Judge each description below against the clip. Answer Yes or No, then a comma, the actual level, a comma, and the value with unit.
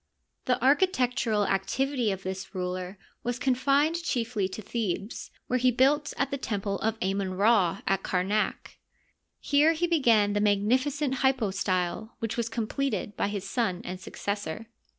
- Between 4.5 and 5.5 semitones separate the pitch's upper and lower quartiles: Yes, average, 5.1 semitones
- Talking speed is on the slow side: No, average, 150 wpm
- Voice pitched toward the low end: No, high, 220 Hz